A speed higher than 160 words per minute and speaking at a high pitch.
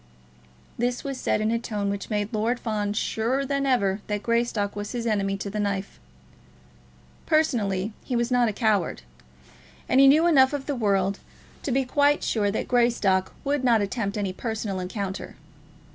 Yes: average, 175 wpm; high, 220 Hz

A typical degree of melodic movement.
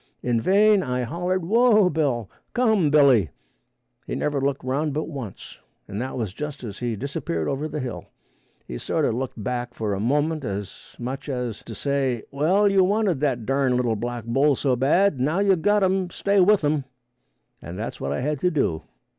No: wide, 6.4 semitones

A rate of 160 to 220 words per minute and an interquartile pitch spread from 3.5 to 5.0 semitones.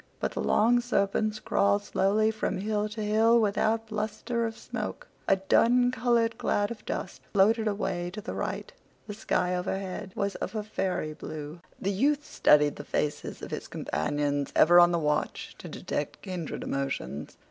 Yes: average, 170 wpm; average, 3.9 semitones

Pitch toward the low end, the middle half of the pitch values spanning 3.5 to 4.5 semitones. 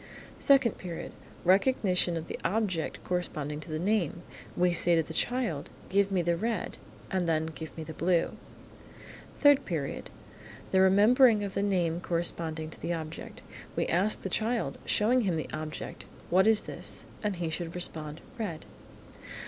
No: medium, 180 Hz; average, 4.1 semitones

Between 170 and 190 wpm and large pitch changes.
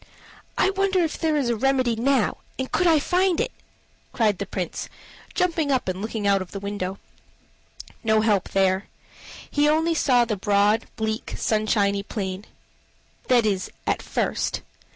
No: average, 150 wpm; wide, 6.7 semitones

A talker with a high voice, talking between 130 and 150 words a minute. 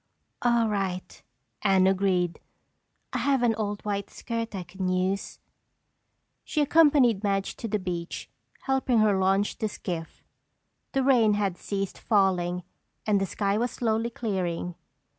Yes: high, 200 Hz; average, 140 wpm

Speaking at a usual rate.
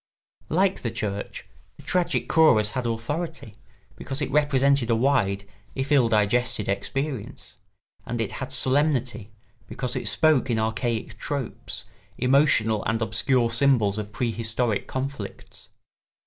No: slow, 125 wpm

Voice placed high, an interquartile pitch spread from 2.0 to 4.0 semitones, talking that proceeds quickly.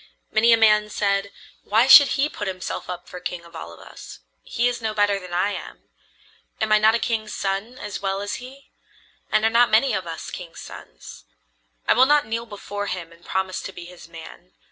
Yes: high, 205 Hz; average, 3.7 semitones; fast, 215 wpm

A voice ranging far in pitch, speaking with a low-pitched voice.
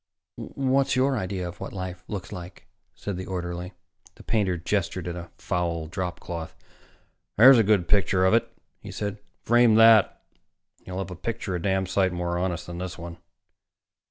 No: average, 2.9 semitones; very low, 95 Hz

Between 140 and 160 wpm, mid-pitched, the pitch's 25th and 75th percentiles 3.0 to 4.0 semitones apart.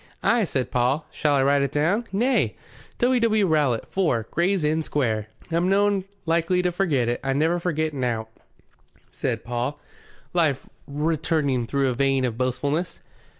No: average, 155 wpm; medium, 150 Hz; average, 5.3 semitones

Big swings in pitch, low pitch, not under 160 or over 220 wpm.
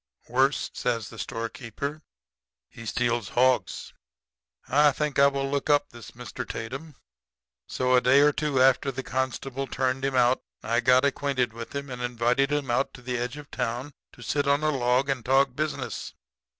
No: narrow, 2.4 semitones; low, 130 Hz; average, 175 wpm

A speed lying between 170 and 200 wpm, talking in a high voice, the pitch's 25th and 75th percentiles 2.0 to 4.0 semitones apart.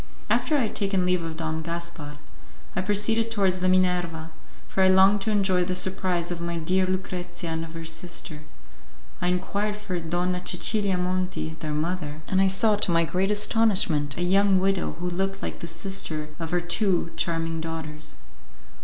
No: average, 180 wpm; medium, 180 Hz; average, 2.7 semitones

